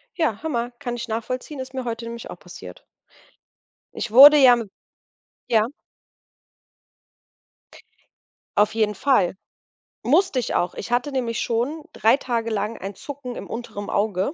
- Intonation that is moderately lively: Yes, average, 3.0 semitones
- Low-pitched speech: No, high, 235 Hz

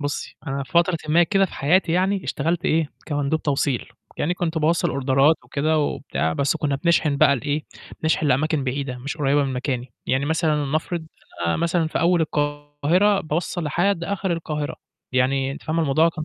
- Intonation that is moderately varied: Yes, average, 3.2 semitones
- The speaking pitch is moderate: Yes, medium, 155 Hz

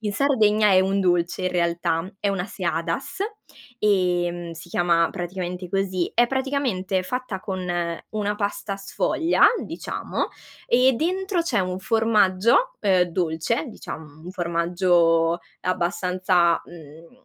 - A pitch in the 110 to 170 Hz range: No, medium, 185 Hz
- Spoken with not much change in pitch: No, average, 3.6 semitones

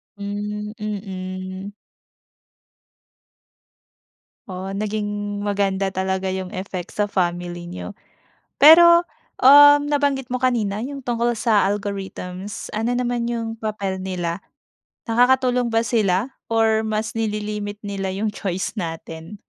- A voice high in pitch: Yes, high, 205 Hz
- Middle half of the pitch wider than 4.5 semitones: No, average, 3.5 semitones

